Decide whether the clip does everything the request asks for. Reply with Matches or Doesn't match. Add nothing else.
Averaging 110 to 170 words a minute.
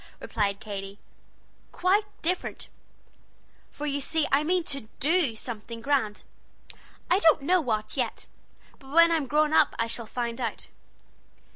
Matches